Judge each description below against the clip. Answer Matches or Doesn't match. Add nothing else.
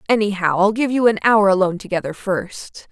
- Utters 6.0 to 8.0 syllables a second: Doesn't match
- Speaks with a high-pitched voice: Matches